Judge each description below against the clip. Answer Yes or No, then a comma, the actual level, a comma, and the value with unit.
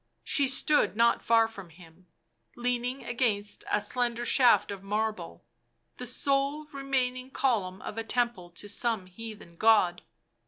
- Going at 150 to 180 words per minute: No, slow, 135 wpm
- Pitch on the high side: Yes, high, 225 Hz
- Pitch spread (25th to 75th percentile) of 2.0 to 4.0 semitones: Yes, average, 3.7 semitones